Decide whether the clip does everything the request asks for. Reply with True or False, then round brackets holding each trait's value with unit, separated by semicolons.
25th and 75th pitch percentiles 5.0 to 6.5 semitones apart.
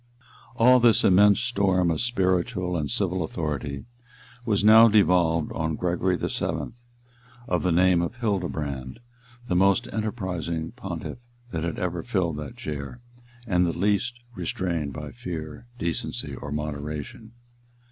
False (4.4 semitones)